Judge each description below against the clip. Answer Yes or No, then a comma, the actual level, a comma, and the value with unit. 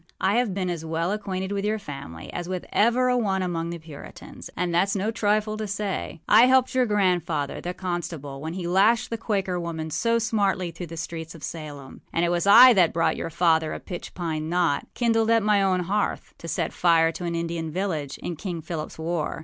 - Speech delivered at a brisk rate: Yes, fast, 215 wpm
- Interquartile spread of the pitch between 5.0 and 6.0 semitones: No, average, 3.9 semitones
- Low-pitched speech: No, medium, 180 Hz